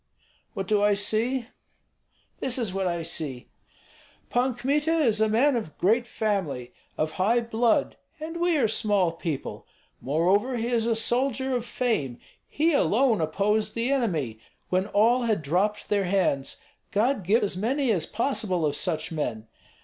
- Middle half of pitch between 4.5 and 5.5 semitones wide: Yes, average, 5.2 semitones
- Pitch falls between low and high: No, high, 215 Hz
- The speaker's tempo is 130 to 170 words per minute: Yes, average, 155 wpm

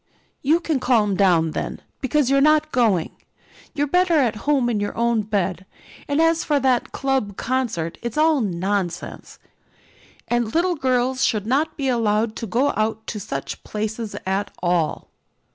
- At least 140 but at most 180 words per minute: Yes, average, 160 wpm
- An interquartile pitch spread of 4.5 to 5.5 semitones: Yes, average, 5.2 semitones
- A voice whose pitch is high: Yes, high, 235 Hz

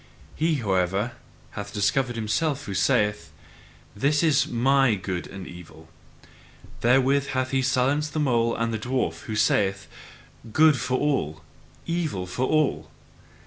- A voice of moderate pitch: No, low, 125 Hz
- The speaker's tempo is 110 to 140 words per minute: Yes, slow, 135 wpm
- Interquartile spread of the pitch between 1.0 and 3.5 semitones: No, wide, 5.4 semitones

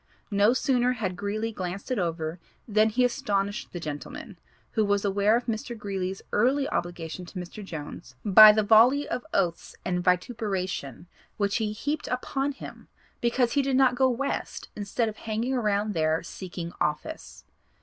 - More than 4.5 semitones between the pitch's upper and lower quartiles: Yes, average, 4.9 semitones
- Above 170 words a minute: No, average, 160 wpm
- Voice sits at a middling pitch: No, high, 210 Hz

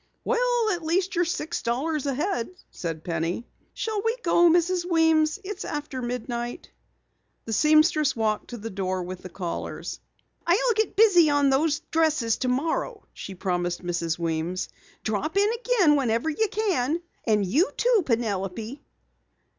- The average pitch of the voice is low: No, very high, 290 Hz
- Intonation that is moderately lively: No, wide, 8.6 semitones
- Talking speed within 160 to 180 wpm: No, average, 145 wpm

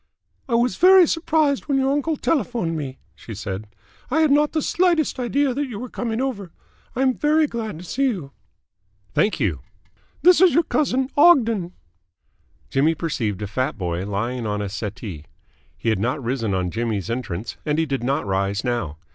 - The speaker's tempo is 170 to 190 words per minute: Yes, average, 180 wpm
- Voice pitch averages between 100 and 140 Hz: No, medium, 165 Hz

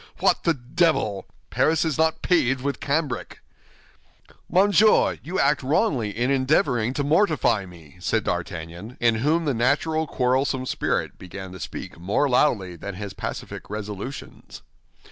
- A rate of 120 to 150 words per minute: Yes, average, 140 wpm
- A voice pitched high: No, low, 130 Hz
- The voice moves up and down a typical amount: No, wide, 7.1 semitones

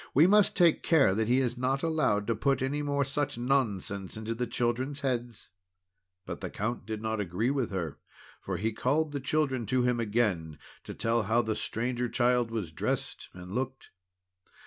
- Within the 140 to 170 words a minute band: No, average, 185 wpm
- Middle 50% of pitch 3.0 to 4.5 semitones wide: Yes, average, 3.9 semitones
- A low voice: Yes, low, 120 Hz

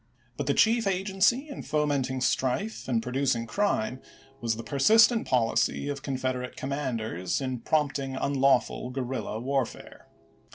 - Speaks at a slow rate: Yes, slow, 125 wpm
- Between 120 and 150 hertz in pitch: Yes, low, 135 Hz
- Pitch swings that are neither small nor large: Yes, average, 3.1 semitones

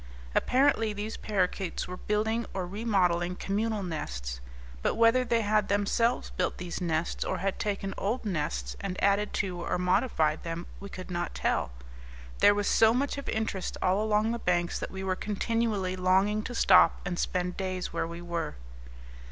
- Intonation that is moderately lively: Yes, average, 3.3 semitones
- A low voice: No, high, 195 Hz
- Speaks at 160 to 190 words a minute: Yes, average, 170 wpm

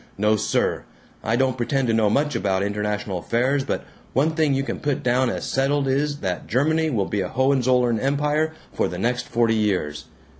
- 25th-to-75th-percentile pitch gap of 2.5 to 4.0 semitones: No, average, 4.9 semitones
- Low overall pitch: Yes, low, 125 Hz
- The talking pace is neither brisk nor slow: Yes, average, 190 wpm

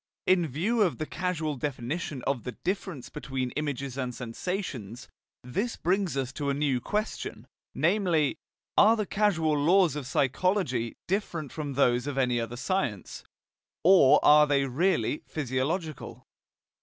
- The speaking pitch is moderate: Yes, medium, 150 Hz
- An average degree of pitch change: No, wide, 5.8 semitones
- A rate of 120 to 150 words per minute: Yes, average, 140 wpm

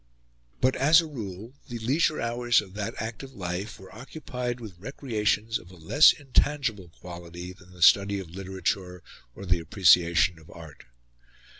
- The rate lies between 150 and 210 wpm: Yes, average, 155 wpm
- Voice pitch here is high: No, low, 100 Hz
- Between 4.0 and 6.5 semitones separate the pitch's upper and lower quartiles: Yes, wide, 5.4 semitones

